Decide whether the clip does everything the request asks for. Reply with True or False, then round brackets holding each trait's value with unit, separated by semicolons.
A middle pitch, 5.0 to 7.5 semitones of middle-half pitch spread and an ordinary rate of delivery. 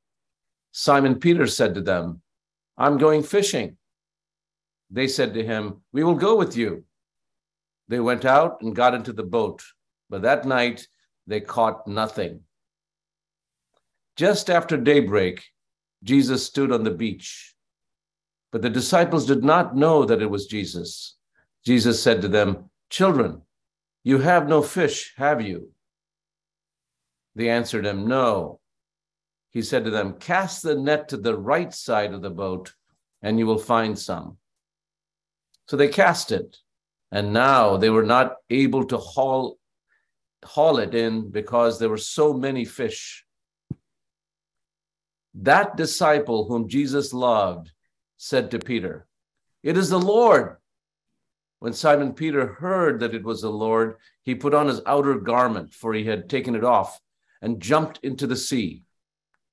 False (125 Hz; 5.3 semitones; 145 wpm)